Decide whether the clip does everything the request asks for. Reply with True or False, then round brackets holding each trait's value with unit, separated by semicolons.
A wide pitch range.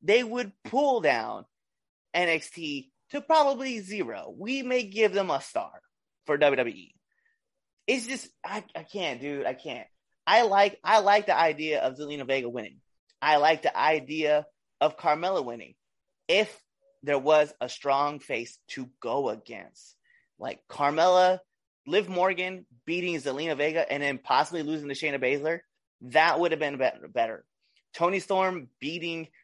True (5.9 semitones)